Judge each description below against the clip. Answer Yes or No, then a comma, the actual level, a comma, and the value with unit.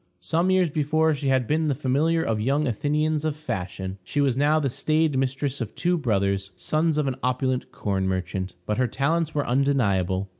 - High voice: No, low, 135 Hz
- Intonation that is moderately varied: No, wide, 6.4 semitones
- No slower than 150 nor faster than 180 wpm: No, average, 190 wpm